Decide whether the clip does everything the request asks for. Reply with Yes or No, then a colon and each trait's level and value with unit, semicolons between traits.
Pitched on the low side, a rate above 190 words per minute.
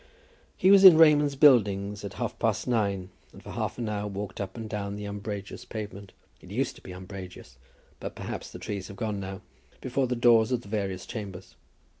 Yes: low, 105 Hz; average, 200 wpm